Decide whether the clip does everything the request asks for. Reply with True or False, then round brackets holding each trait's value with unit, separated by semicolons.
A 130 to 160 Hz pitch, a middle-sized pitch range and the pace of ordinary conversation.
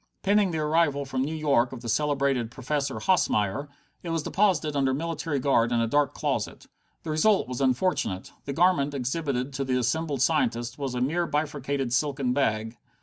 True (140 Hz; 3.6 semitones; 175 wpm)